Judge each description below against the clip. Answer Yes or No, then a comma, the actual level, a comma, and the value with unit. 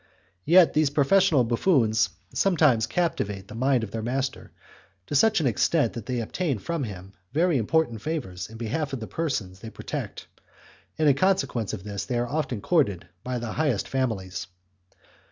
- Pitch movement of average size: No, wide, 6.1 semitones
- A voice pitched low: Yes, low, 125 Hz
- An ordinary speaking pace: Yes, average, 170 wpm